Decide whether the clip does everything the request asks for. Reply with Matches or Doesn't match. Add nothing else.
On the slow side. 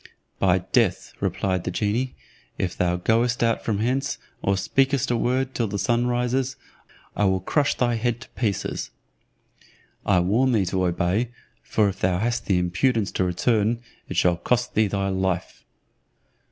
Doesn't match